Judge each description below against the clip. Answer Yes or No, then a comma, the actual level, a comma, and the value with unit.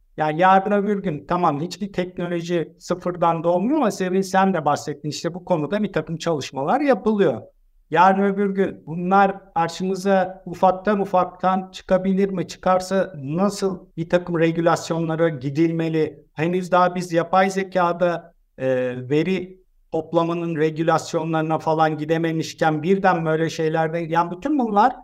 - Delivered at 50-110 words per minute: No, average, 125 wpm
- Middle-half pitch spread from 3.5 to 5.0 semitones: No, average, 2.7 semitones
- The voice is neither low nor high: Yes, medium, 175 Hz